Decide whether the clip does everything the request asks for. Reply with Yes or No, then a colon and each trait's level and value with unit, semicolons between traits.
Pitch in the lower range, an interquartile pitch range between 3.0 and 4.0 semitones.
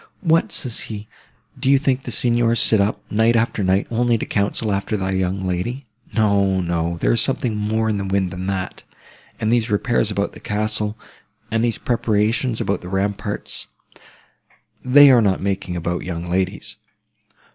Yes: low, 105 Hz; average, 3.5 semitones